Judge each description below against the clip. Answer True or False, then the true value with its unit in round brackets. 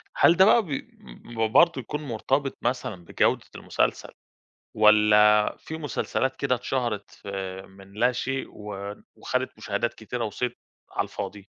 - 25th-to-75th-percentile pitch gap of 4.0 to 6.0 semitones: True (4.6 semitones)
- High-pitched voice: False (115 Hz)